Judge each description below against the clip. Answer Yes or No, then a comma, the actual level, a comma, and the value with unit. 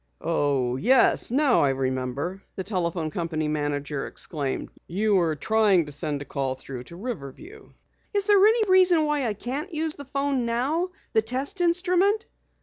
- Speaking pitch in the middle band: No, high, 215 Hz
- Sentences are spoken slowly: No, average, 155 wpm